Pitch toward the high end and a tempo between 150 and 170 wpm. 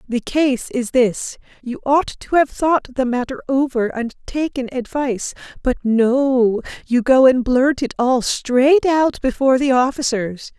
Yes: very high, 255 Hz; average, 160 wpm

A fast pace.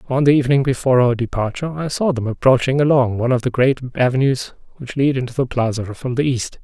Yes: fast, 215 wpm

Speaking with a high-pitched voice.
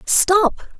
Yes: very high, 410 Hz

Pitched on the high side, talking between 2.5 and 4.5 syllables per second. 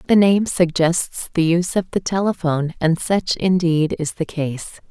No: medium, 170 Hz; 4.4 syllables/s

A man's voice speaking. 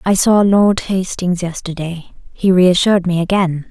No: female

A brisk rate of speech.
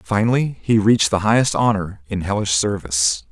No: average, 165 wpm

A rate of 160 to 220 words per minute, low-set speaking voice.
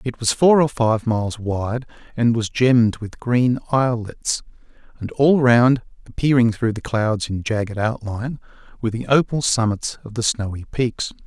Yes: average, 165 wpm; low, 115 Hz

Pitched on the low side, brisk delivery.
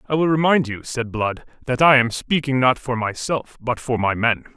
Yes: low, 125 Hz; fast, 225 wpm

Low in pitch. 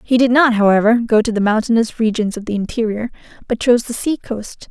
No: high, 225 Hz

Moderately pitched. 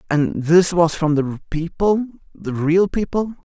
Yes: medium, 170 Hz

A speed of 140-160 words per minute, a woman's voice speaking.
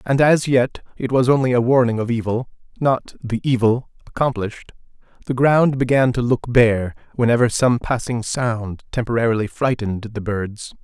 No: average, 155 wpm; male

